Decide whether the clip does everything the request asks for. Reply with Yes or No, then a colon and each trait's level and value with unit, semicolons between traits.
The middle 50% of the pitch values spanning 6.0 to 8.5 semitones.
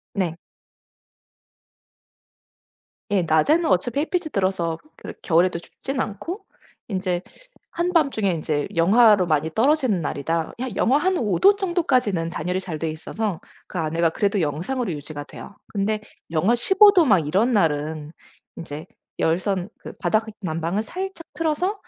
Yes: wide, 7.8 semitones